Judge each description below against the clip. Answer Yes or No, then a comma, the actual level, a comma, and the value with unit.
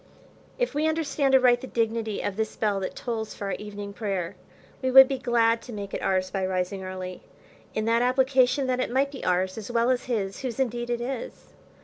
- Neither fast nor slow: No, fast, 215 wpm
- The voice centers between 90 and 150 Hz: No, high, 230 Hz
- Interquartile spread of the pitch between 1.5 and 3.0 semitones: No, average, 4.3 semitones